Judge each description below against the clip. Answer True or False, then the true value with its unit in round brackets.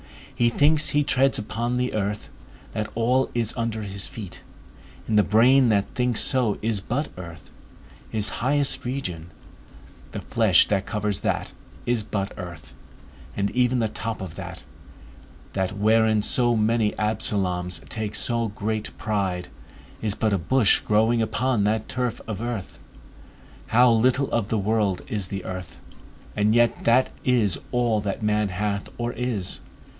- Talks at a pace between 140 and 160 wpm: True (150 wpm)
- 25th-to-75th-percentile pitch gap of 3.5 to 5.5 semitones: False (2.9 semitones)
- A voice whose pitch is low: True (110 Hz)